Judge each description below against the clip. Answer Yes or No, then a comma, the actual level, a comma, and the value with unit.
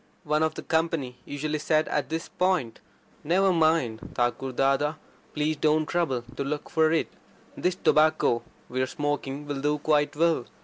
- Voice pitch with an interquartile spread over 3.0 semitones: No, narrow, 2.6 semitones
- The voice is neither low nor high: Yes, medium, 150 Hz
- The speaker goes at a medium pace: Yes, average, 160 wpm